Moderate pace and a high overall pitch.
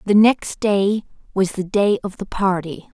Yes: average, 180 wpm; high, 195 Hz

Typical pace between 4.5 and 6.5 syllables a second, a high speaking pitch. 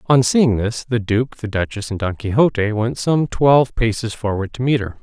No: 5.0 syllables/s; low, 115 Hz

